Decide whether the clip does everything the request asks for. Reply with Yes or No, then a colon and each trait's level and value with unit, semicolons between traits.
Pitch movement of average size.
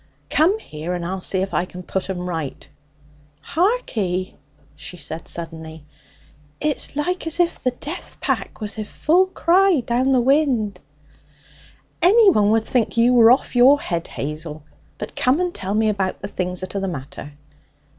No: wide, 8.6 semitones